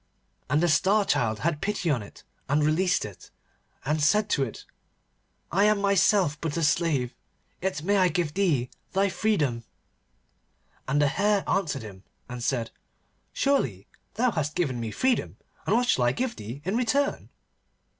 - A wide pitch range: Yes, wide, 7.1 semitones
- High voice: No, medium, 160 Hz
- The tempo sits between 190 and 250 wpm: No, average, 165 wpm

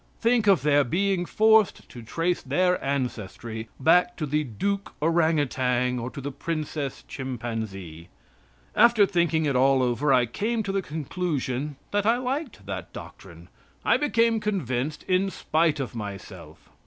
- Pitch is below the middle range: No, medium, 150 Hz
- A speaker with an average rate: Yes, average, 150 wpm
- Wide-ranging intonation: Yes, wide, 7.5 semitones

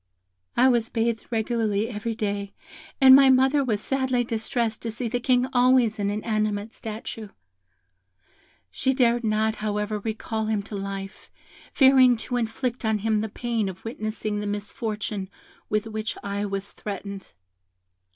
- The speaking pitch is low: No, high, 220 Hz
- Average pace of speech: Yes, average, 145 wpm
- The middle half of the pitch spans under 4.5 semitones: Yes, narrow, 2.6 semitones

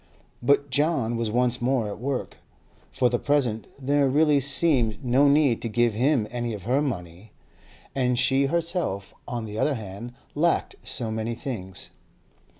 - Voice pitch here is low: Yes, low, 125 Hz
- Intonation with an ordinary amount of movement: Yes, average, 4.0 semitones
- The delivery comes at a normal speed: Yes, average, 155 wpm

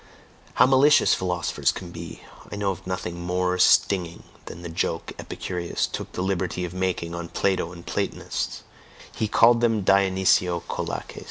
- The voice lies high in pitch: No, very low, 90 Hz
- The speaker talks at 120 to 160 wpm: Yes, average, 155 wpm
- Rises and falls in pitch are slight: Yes, narrow, 2.0 semitones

